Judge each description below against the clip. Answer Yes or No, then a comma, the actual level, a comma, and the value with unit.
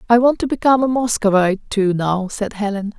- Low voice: No, high, 215 Hz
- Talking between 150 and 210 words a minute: Yes, average, 200 wpm